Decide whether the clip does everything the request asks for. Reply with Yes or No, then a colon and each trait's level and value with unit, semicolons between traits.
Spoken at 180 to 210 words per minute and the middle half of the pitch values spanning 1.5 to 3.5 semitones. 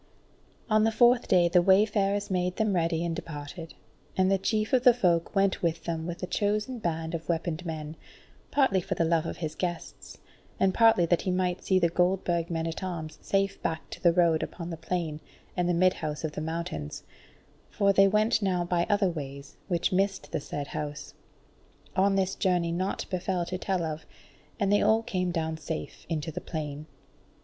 Yes: average, 190 wpm; average, 3.1 semitones